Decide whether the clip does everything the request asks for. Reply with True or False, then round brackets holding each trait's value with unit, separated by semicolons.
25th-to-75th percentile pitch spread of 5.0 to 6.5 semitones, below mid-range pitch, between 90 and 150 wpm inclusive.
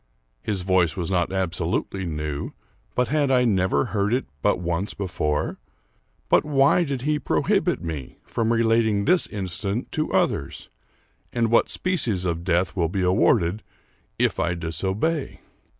True (5.3 semitones; 95 Hz; 145 wpm)